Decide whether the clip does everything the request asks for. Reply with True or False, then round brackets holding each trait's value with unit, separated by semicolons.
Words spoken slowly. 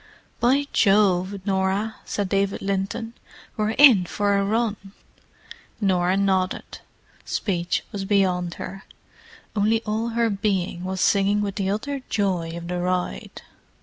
True (130 wpm)